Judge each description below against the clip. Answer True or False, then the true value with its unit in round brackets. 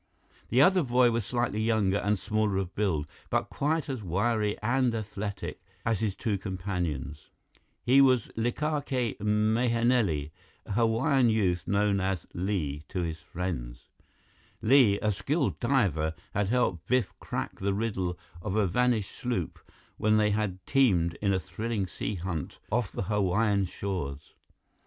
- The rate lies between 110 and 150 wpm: True (145 wpm)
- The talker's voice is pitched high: False (105 Hz)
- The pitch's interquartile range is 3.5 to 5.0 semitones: True (4.1 semitones)